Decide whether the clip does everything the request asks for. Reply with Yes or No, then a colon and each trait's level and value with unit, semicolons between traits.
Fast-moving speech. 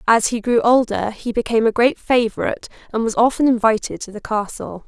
No: average, 195 wpm